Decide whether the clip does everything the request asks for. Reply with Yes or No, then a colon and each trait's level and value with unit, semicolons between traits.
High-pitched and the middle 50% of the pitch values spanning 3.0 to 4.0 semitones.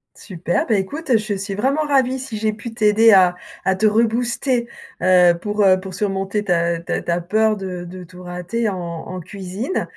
Yes: high, 200 Hz; average, 3.7 semitones